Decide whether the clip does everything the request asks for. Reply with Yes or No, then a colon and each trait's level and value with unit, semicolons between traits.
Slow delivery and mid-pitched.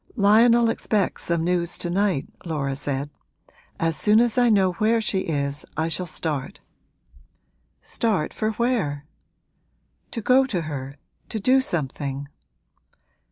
Yes: slow, 130 wpm; medium, 180 Hz